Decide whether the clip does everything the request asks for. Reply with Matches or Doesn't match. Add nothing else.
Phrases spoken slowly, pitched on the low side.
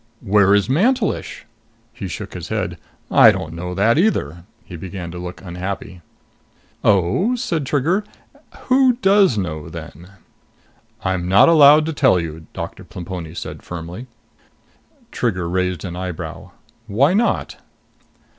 Matches